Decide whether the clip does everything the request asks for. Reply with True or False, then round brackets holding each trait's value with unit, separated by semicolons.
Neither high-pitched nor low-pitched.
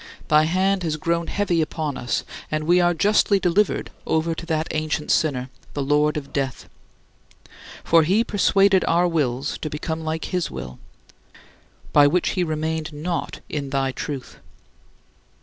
True (160 Hz)